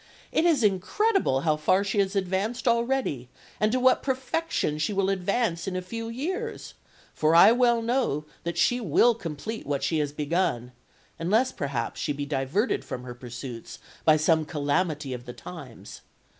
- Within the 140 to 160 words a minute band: No, average, 170 wpm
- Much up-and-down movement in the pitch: Yes, wide, 8.1 semitones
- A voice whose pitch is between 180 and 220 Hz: Yes, medium, 185 Hz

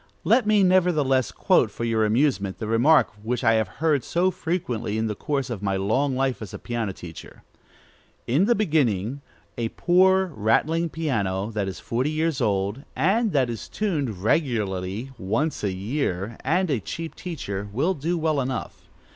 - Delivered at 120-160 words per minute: No, average, 170 wpm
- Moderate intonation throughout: No, wide, 7.1 semitones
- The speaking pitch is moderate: No, low, 130 Hz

